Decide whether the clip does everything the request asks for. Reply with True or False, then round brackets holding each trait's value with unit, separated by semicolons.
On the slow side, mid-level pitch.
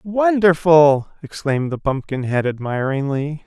True (85 wpm; 150 Hz)